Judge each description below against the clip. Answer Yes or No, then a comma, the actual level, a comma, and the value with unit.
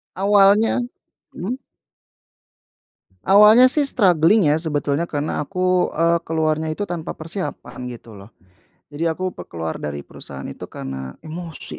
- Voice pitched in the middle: Yes, medium, 165 Hz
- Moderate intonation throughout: Yes, average, 4.9 semitones